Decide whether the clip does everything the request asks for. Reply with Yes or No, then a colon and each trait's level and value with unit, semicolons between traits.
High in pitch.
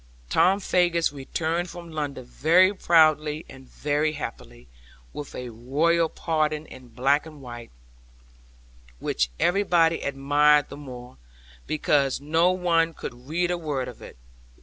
No: medium, 150 Hz